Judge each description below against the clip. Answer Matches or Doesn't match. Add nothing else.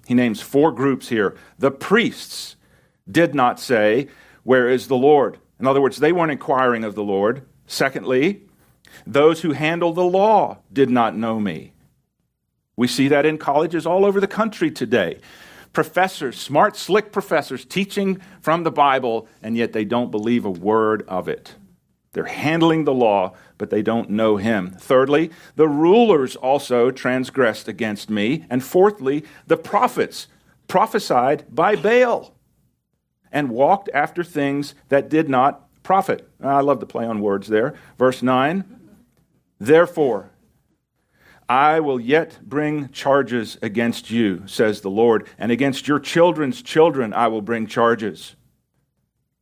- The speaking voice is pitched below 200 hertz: Matches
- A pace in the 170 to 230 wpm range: Doesn't match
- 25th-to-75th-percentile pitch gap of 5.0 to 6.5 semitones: Matches